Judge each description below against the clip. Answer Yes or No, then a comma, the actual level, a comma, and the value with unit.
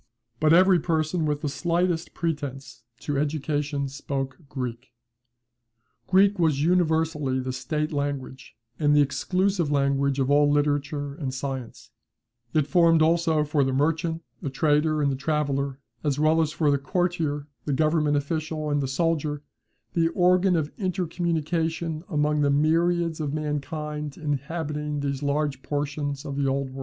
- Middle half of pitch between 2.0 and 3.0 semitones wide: Yes, narrow, 2.4 semitones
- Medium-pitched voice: Yes, medium, 150 Hz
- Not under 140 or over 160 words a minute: Yes, average, 150 wpm